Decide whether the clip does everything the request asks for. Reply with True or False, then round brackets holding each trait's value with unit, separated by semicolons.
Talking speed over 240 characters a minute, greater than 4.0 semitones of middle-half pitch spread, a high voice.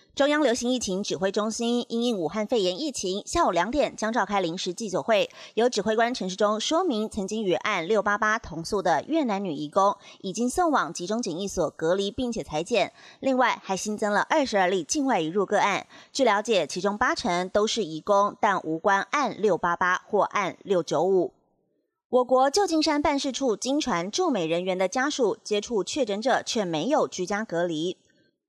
True (265 characters per minute; 5.3 semitones; 215 Hz)